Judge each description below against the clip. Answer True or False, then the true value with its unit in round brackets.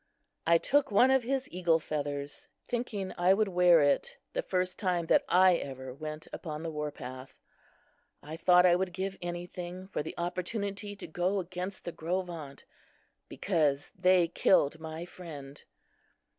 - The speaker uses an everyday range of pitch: True (3.3 semitones)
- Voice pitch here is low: False (175 Hz)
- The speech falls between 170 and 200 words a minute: False (155 wpm)